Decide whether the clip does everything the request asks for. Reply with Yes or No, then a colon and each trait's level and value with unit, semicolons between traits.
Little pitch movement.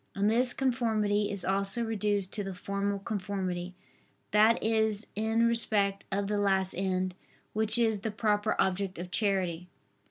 Yes: narrow, 2.2 semitones